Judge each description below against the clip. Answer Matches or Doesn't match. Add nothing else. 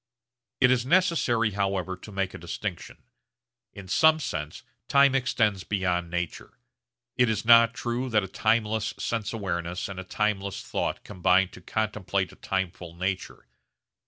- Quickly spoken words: Doesn't match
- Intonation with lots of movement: Doesn't match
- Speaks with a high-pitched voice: Doesn't match